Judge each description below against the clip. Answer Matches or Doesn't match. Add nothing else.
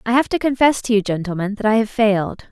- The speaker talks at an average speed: Doesn't match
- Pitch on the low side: Doesn't match